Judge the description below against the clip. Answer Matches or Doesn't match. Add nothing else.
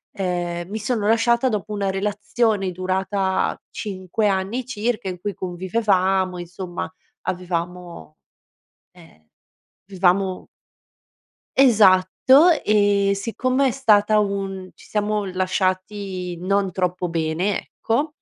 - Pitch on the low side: Doesn't match